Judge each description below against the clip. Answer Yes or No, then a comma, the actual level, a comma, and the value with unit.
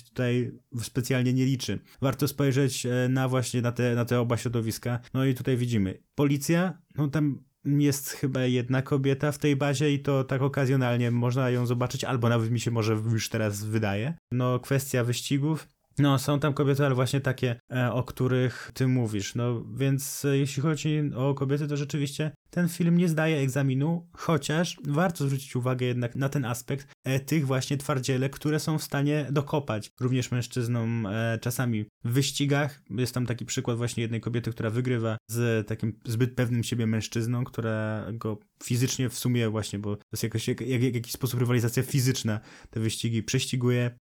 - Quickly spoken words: Yes, fast, 170 wpm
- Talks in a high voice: No, low, 130 Hz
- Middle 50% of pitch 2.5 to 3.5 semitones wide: Yes, average, 3.0 semitones